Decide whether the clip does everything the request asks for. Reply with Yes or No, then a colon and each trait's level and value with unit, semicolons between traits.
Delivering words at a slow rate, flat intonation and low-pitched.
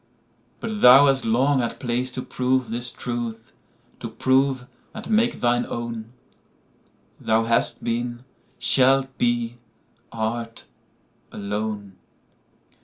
Yes: slow, 95 wpm; narrow, 2.3 semitones; low, 120 Hz